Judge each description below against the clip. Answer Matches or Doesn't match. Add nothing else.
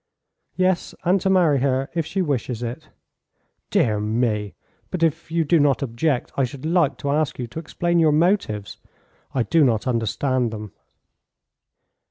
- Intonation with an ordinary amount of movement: Doesn't match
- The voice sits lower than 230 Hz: Matches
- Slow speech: Doesn't match